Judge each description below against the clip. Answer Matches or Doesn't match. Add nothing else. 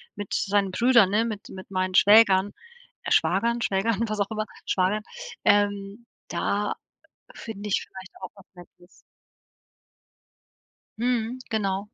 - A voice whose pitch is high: Matches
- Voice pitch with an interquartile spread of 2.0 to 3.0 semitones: Matches